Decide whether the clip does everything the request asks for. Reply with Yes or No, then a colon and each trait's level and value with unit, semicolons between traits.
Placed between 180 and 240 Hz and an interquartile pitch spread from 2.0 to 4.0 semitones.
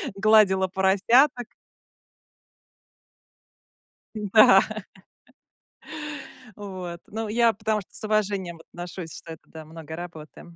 Yes: high, 190 Hz; average, 3.7 semitones